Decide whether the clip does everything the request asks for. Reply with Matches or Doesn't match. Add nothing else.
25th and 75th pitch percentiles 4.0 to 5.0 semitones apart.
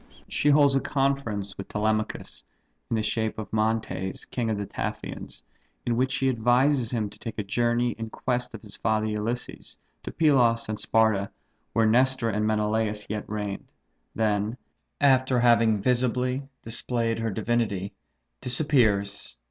Doesn't match